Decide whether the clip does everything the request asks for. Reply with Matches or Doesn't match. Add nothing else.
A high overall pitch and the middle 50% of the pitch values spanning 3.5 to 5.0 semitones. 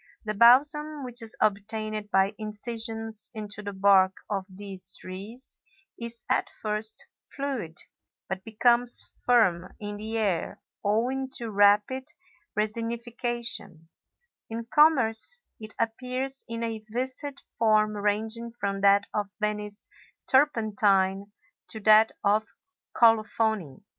Doesn't match